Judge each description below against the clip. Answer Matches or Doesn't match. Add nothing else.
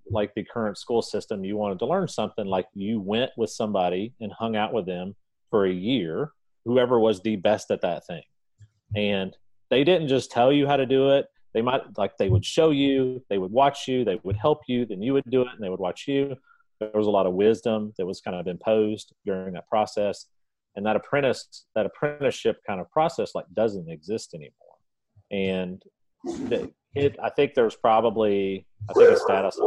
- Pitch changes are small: Doesn't match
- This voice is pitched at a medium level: Doesn't match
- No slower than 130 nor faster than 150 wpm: Doesn't match